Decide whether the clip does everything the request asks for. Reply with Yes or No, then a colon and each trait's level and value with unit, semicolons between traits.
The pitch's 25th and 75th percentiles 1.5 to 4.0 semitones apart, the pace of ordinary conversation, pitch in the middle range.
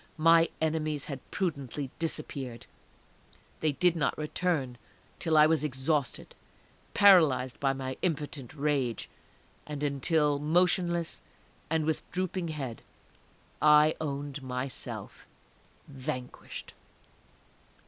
No: average, 3.1 semitones; slow, 95 wpm; medium, 150 Hz